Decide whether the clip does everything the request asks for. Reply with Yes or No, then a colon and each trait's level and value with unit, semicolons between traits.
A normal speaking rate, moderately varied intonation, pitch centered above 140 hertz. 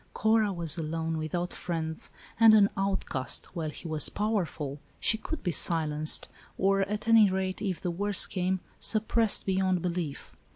Yes: average, 160 wpm; average, 4.0 semitones; medium, 185 Hz